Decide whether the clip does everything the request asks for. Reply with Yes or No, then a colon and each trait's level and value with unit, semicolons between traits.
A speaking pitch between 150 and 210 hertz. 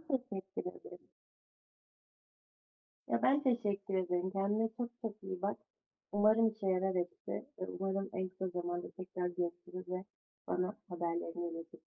Yes: high, 190 Hz